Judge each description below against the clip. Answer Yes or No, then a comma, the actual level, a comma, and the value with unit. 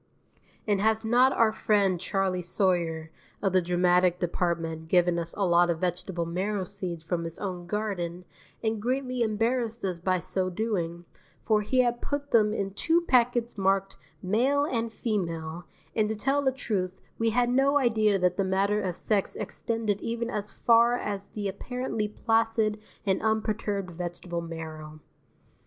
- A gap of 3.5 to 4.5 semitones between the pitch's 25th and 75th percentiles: Yes, average, 4.2 semitones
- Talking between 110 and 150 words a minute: No, average, 160 wpm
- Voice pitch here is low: No, high, 200 Hz